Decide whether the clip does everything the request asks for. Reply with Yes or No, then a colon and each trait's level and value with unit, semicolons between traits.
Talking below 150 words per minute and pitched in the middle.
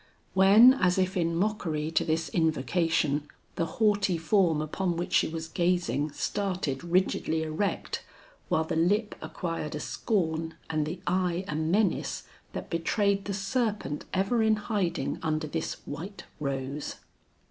Yes: average, 140 wpm; medium, 170 Hz